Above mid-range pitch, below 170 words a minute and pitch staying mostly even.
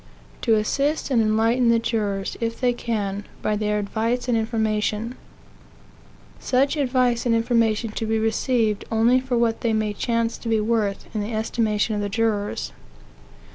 Yes: high, 225 Hz; average, 160 wpm; narrow, 1.9 semitones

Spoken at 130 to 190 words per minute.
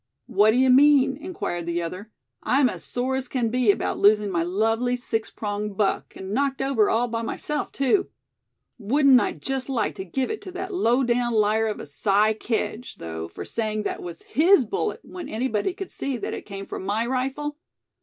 No: average, 200 wpm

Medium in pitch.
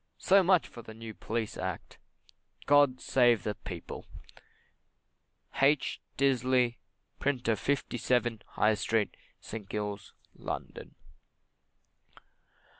No: low, 120 Hz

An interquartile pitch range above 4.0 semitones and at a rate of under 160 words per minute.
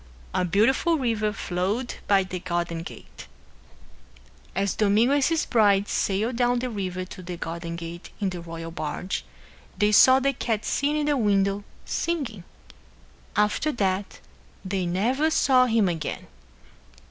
Yes: average, 5.2 semitones; average, 145 wpm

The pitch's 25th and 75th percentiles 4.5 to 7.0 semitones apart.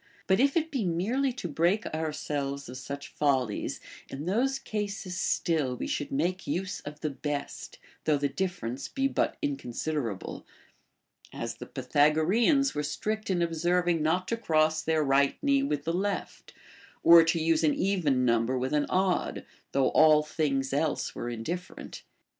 Yes: average, 5.1 semitones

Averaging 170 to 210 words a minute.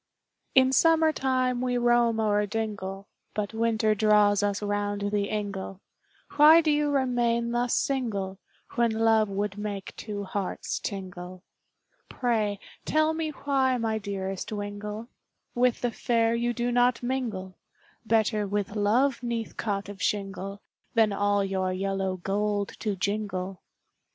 No: slow, 135 wpm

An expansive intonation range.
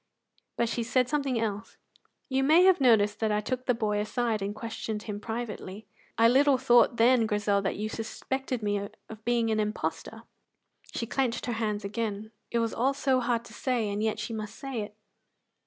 No: average, 2.9 semitones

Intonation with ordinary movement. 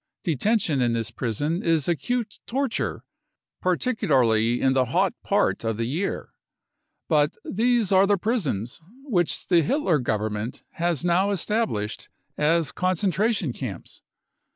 No: wide, 8.4 semitones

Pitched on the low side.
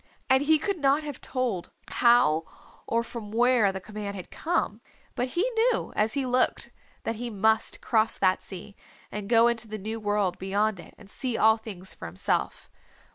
No: high, 220 Hz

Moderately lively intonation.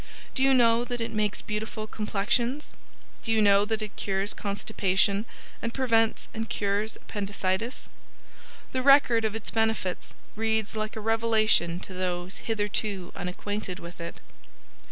No: narrow, 2.2 semitones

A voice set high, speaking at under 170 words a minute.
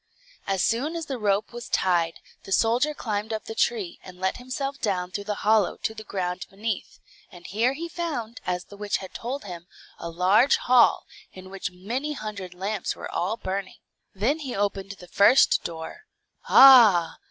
No: high, 210 Hz; average, 180 wpm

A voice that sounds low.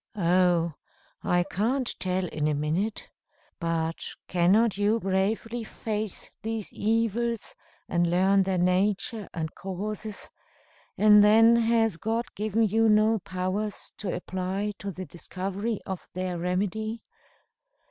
No: high, 200 Hz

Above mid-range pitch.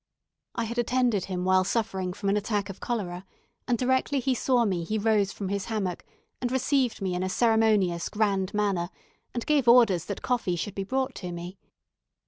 Yes: high, 205 Hz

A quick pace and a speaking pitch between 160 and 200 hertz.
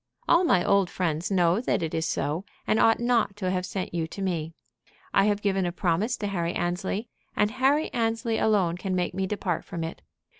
Yes: fast, 210 wpm; high, 190 Hz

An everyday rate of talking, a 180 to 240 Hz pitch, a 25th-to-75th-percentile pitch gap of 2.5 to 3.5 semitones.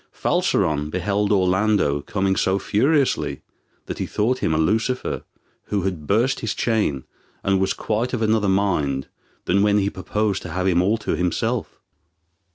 No: average, 160 wpm; low, 100 Hz; average, 3.1 semitones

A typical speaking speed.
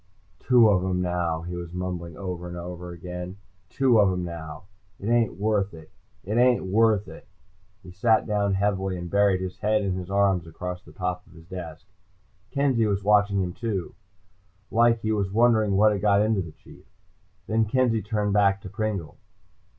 Yes: average, 180 wpm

